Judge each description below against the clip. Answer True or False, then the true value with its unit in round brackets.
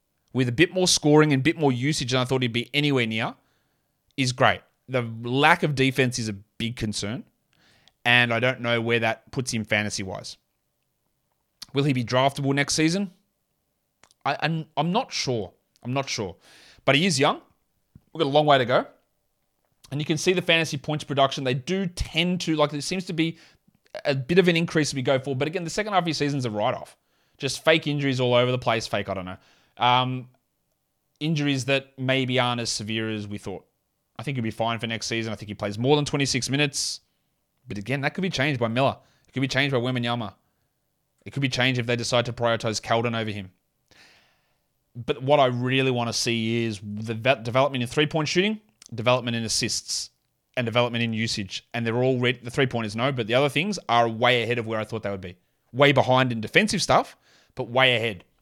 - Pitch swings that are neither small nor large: True (3.9 semitones)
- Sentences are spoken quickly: True (225 wpm)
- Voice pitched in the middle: False (130 Hz)